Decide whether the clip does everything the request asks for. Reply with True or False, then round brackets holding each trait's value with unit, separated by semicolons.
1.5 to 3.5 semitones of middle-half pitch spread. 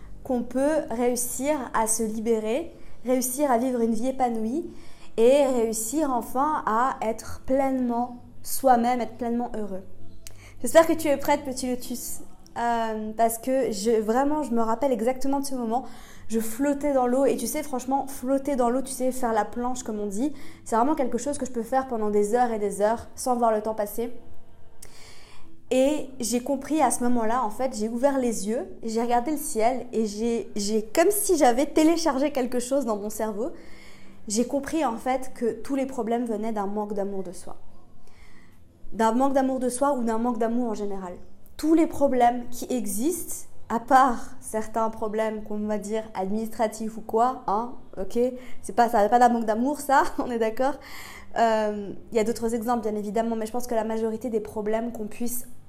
True (3.0 semitones)